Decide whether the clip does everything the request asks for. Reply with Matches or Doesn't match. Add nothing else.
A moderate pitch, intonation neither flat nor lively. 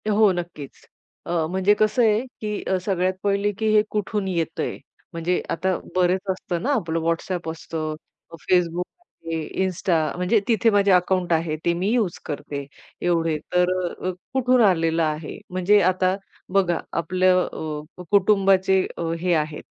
Matches